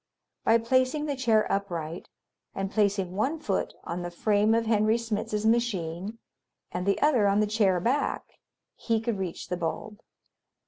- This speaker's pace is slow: No, average, 155 wpm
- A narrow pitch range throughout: No, average, 3.3 semitones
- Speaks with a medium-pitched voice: No, high, 210 Hz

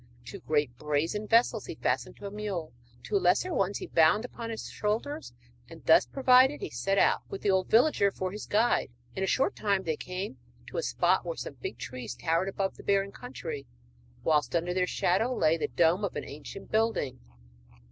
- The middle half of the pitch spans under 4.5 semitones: No, average, 5.3 semitones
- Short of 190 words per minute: No, average, 200 wpm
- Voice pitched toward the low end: No, high, 195 Hz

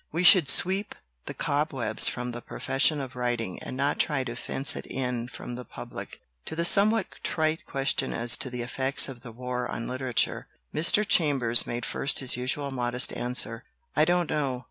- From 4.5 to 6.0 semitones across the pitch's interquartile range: No, average, 3.7 semitones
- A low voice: Yes, low, 130 Hz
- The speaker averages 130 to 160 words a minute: No, average, 185 wpm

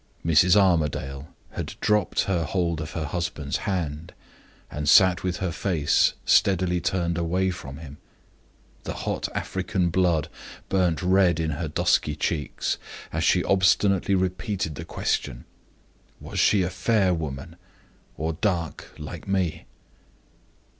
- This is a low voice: Yes, very low, 85 Hz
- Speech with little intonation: No, average, 3.1 semitones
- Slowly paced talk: Yes, slow, 130 wpm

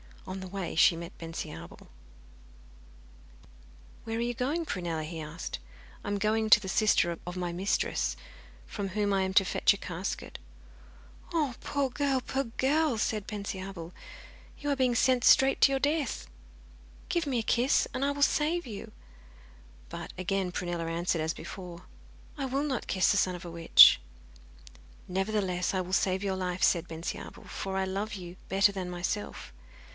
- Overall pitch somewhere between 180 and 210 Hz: Yes, high, 190 Hz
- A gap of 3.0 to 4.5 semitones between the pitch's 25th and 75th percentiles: No, wide, 5.6 semitones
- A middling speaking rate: Yes, average, 165 wpm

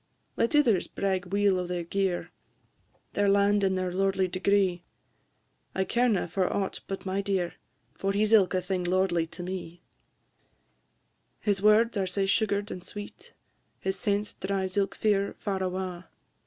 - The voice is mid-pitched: No, high, 195 Hz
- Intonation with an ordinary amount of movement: No, narrow, 1.6 semitones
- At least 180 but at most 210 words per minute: No, average, 155 wpm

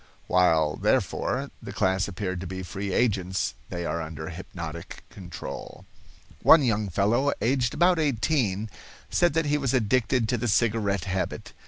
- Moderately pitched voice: No, low, 100 Hz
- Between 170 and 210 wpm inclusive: No, average, 150 wpm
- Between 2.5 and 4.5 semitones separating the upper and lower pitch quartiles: No, average, 5.2 semitones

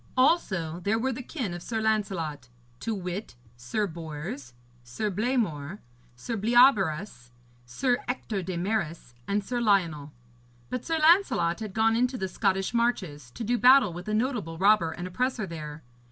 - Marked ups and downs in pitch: Yes, wide, 6.2 semitones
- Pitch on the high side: Yes, high, 200 Hz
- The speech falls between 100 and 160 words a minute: Yes, average, 155 wpm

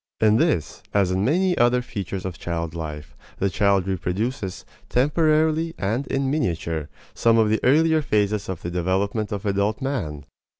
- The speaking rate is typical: Yes, average, 160 wpm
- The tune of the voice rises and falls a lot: Yes, wide, 6.4 semitones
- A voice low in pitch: Yes, low, 105 Hz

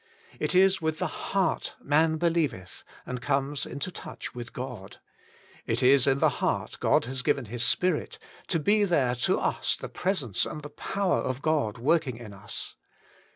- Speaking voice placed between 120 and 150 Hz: Yes, medium, 140 Hz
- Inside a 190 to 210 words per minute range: No, average, 170 wpm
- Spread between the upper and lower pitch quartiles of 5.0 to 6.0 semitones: Yes, wide, 5.4 semitones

